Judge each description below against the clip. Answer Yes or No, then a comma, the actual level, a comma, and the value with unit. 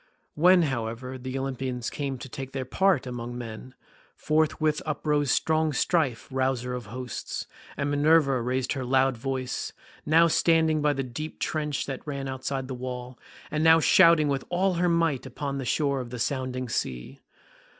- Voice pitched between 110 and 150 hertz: Yes, low, 135 Hz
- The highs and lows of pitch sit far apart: No, average, 3.3 semitones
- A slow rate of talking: No, average, 165 wpm